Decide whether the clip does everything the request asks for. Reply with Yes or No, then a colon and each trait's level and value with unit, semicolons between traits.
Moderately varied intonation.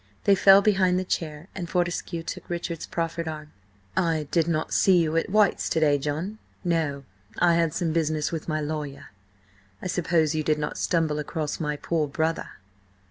No: narrow, 2.3 semitones